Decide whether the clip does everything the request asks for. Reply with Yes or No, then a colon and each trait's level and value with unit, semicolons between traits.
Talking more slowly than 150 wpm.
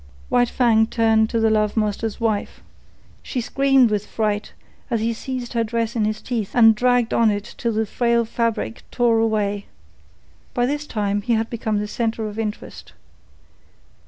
No: average, 170 wpm